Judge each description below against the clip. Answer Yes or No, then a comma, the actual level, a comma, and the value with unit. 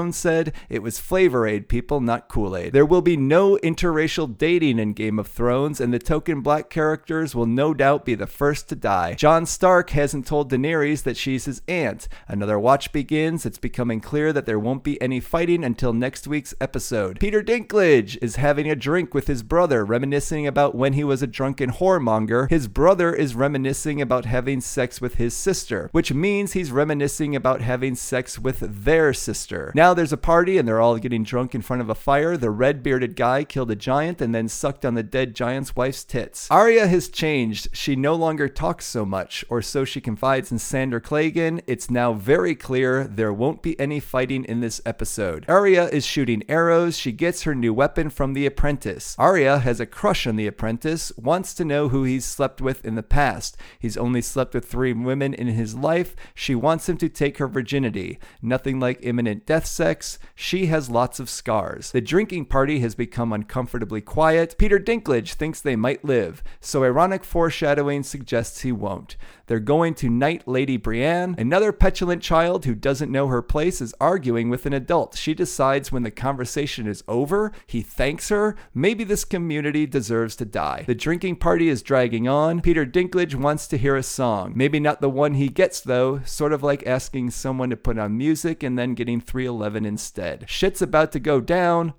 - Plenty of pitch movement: No, average, 4.5 semitones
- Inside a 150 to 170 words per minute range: No, average, 195 wpm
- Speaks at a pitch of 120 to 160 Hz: Yes, medium, 140 Hz